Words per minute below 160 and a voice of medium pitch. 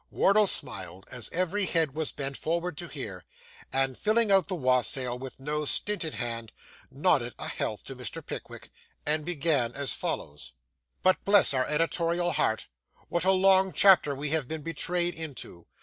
No: average, 165 wpm; medium, 155 Hz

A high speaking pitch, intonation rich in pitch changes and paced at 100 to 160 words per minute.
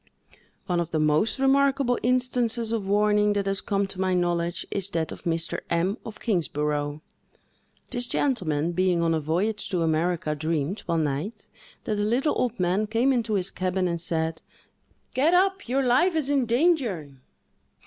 No: high, 195 Hz; wide, 6.2 semitones; average, 170 wpm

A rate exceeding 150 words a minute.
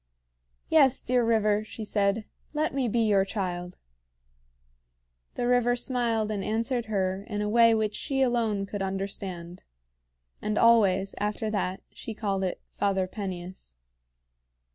No: slow, 135 wpm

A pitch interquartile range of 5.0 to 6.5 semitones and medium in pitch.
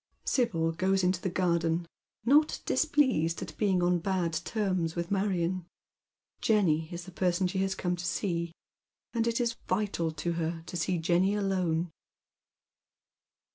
No: narrow, 2.6 semitones; medium, 180 Hz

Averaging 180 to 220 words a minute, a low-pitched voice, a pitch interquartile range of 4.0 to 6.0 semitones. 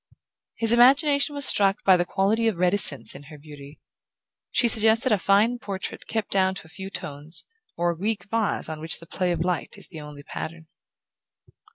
No: average, 190 wpm; high, 190 Hz; wide, 5.4 semitones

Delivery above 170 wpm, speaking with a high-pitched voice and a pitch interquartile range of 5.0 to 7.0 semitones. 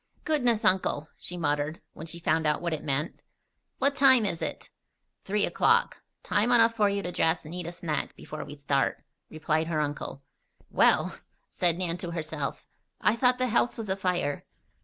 No: average, 180 wpm; medium, 175 Hz; wide, 5.5 semitones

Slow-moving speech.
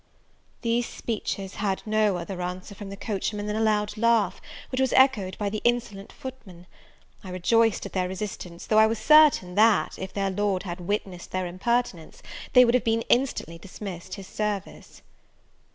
No: average, 170 wpm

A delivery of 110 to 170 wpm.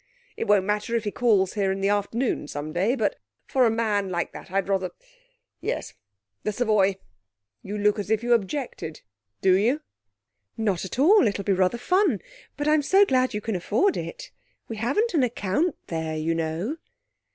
No: average, 185 wpm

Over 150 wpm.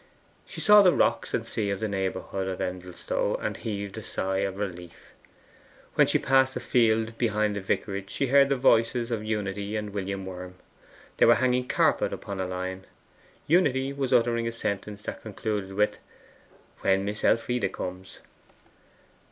Yes: average, 170 wpm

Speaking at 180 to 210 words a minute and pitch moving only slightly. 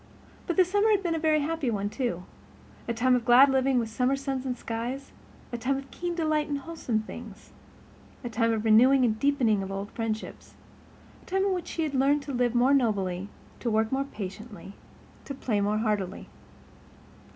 No: average, 190 wpm; average, 4.4 semitones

